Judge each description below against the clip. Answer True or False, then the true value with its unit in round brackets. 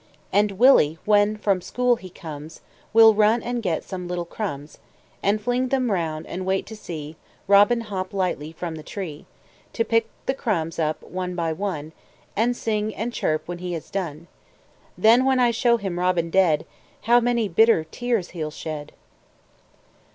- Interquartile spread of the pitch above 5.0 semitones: True (5.4 semitones)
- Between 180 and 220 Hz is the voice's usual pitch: True (190 Hz)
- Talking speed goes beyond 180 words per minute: False (170 wpm)